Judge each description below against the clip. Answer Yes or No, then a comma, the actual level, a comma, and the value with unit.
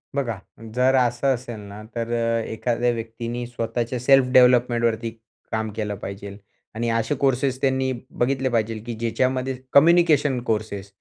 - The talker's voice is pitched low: Yes, low, 120 Hz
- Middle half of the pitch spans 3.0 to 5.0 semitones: No, narrow, 2.5 semitones